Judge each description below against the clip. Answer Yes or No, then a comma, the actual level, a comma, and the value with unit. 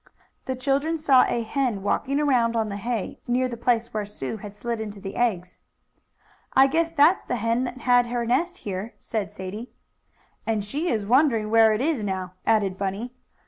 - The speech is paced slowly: No, average, 185 wpm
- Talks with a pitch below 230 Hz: No, high, 235 Hz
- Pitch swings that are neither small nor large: Yes, average, 3.9 semitones